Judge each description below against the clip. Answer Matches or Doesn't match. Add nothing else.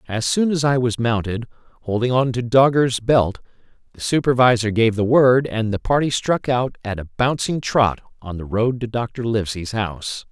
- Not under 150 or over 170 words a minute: Doesn't match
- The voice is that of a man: Matches